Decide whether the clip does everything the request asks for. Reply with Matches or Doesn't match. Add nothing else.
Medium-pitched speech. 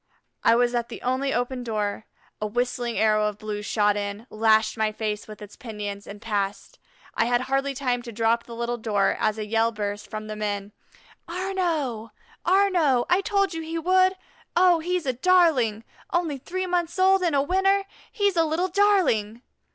Doesn't match